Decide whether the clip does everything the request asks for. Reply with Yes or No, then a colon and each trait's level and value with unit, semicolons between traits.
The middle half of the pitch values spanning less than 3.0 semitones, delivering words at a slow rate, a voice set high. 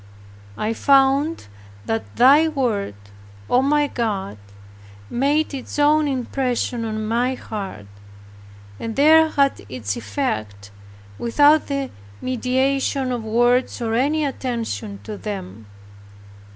No: average, 4.4 semitones; slow, 110 wpm; very high, 250 Hz